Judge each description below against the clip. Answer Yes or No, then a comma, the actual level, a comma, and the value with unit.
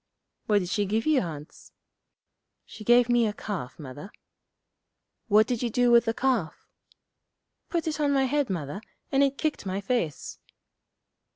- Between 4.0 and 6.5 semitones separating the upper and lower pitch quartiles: Yes, wide, 5.4 semitones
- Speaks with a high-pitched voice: Yes, high, 225 Hz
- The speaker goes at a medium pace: Yes, average, 160 wpm